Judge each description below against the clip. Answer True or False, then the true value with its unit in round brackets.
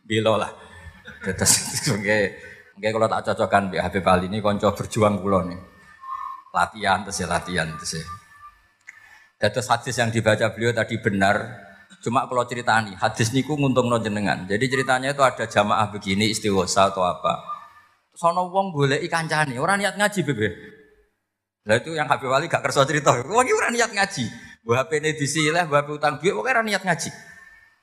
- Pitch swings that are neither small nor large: False (8.4 semitones)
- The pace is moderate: False (155 wpm)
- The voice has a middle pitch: False (120 Hz)